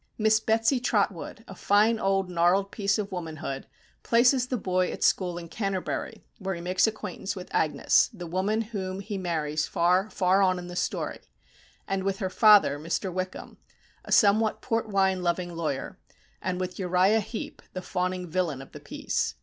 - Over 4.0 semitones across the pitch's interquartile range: No, average, 2.7 semitones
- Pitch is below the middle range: No, medium, 185 Hz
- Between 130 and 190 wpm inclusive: Yes, average, 175 wpm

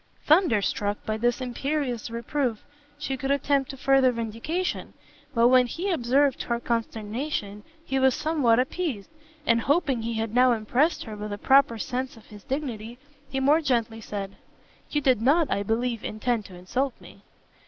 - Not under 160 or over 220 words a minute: Yes, average, 165 wpm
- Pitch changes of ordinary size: Yes, average, 3.8 semitones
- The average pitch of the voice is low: No, high, 245 Hz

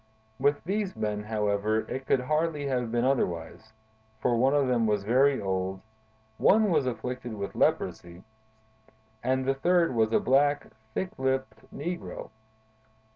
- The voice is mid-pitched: No, low, 130 Hz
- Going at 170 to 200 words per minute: No, average, 140 wpm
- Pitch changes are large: No, average, 4.8 semitones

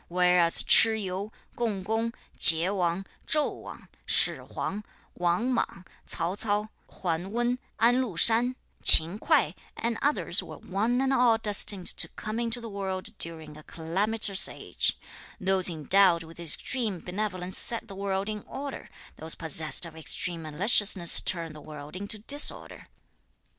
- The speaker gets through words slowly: No, average, 150 wpm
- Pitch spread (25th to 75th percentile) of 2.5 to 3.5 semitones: No, average, 4.7 semitones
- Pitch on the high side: Yes, high, 195 Hz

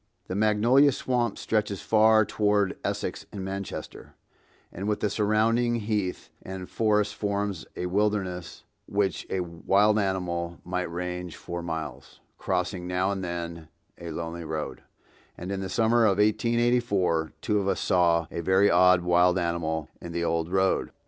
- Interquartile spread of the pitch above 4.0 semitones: No, average, 3.4 semitones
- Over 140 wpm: Yes, average, 150 wpm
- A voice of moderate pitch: No, very low, 95 Hz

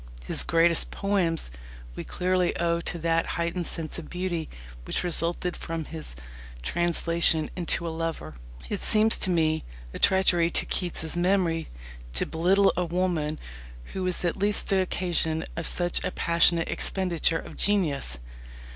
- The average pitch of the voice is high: No, medium, 170 Hz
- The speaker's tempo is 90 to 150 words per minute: Yes, average, 145 wpm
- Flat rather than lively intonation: Yes, narrow, 1.8 semitones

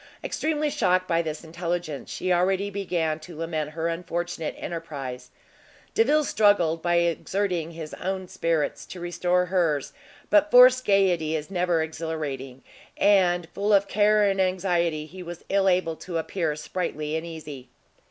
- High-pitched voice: No, medium, 175 Hz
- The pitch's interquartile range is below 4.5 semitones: Yes, average, 3.1 semitones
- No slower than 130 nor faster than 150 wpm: Yes, average, 145 wpm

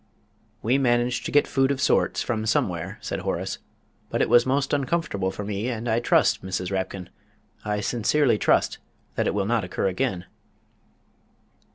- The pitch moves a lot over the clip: No, average, 4.9 semitones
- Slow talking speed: No, average, 165 wpm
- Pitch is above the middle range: No, low, 115 Hz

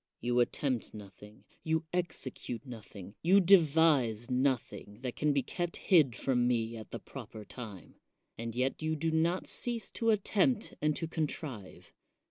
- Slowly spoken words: No, average, 150 wpm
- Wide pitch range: Yes, wide, 6.0 semitones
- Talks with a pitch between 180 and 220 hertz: No, low, 135 Hz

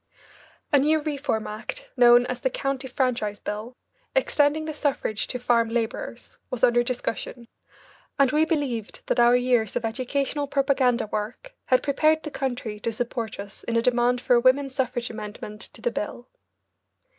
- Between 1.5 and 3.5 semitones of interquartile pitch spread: Yes, average, 3.1 semitones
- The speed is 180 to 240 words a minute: No, average, 165 wpm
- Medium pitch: No, high, 245 Hz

